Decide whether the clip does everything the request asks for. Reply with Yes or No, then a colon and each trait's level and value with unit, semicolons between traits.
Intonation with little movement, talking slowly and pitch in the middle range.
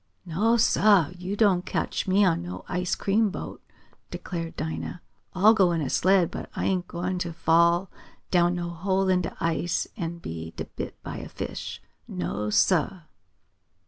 No: narrow, 2.3 semitones; average, 165 wpm; medium, 175 Hz